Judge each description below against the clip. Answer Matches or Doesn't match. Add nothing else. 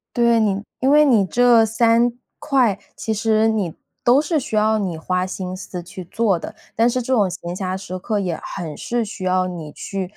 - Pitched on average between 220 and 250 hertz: Doesn't match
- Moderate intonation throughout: Matches